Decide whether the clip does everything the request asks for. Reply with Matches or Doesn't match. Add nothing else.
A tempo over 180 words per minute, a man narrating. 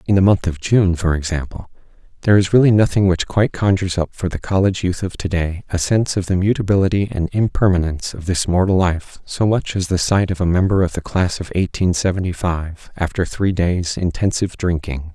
Matches